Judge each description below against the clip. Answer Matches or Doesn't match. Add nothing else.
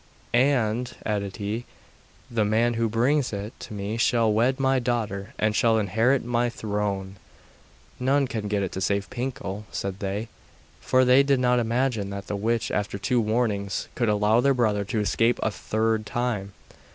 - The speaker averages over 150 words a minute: Matches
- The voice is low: Matches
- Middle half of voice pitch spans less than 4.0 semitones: Matches